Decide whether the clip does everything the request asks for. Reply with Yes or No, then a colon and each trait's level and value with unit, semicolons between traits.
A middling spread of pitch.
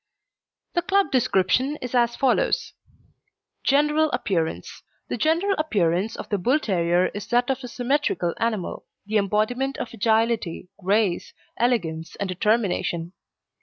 No: wide, 6.2 semitones